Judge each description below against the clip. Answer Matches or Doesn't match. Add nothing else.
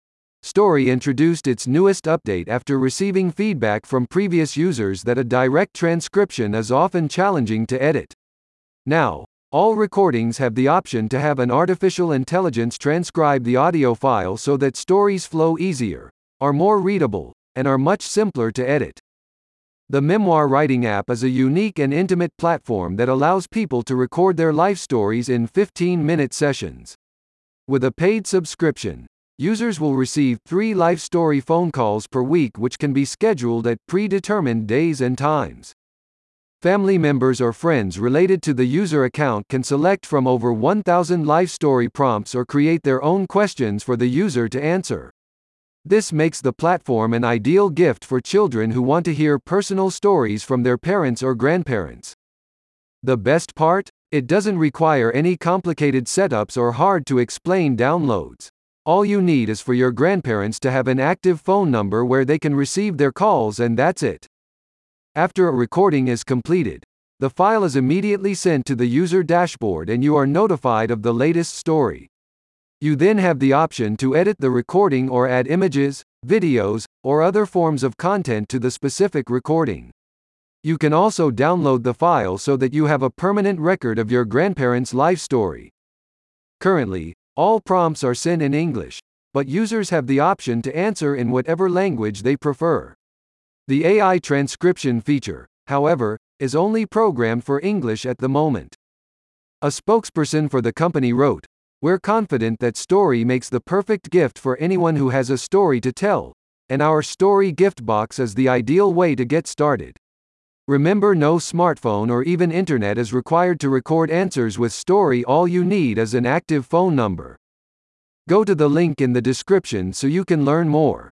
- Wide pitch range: Matches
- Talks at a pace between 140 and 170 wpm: Matches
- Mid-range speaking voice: Matches